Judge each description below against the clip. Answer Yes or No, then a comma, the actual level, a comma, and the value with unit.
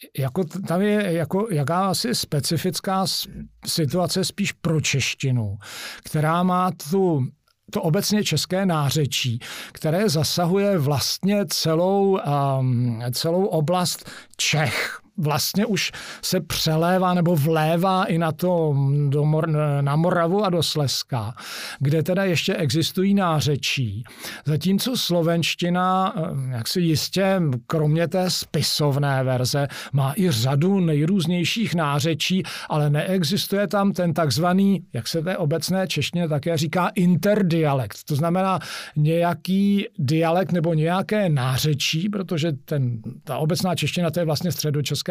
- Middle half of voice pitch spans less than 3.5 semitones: No, average, 4.1 semitones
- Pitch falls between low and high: Yes, medium, 165 Hz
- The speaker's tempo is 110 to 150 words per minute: Yes, average, 120 wpm